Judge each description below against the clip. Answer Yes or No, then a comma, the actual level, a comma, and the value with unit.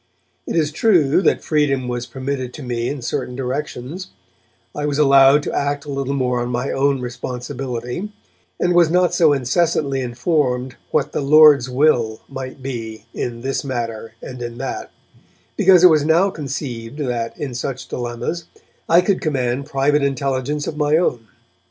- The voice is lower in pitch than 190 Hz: Yes, low, 135 Hz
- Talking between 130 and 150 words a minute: No, average, 165 wpm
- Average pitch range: Yes, average, 3.4 semitones